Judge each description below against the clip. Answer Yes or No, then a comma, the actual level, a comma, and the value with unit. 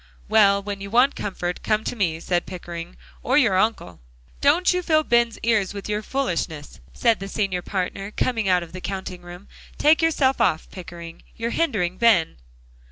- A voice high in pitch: Yes, high, 200 Hz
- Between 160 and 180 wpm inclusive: Yes, average, 175 wpm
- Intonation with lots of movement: No, average, 4.8 semitones